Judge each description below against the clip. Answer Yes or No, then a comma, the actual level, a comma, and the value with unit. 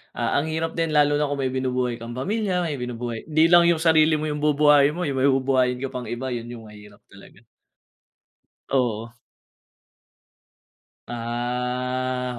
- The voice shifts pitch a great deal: No, average, 3.7 semitones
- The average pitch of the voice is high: No, low, 130 Hz